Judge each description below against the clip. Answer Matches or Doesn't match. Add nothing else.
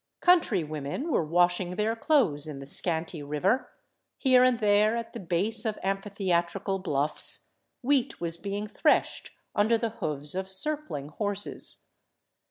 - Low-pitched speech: Doesn't match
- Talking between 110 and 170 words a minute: Matches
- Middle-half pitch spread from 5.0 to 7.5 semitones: Matches